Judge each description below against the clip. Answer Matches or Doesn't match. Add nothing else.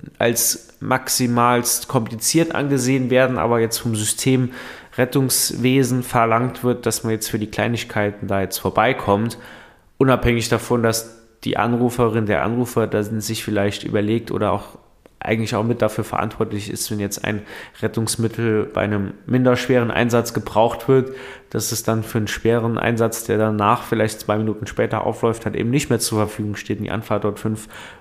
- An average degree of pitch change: Doesn't match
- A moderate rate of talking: Matches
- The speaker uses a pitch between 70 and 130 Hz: Matches